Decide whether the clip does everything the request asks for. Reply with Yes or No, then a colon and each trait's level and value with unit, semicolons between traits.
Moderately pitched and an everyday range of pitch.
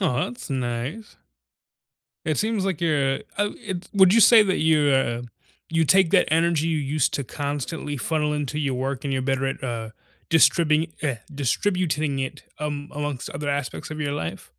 Yes: medium, 150 Hz; average, 3.5 semitones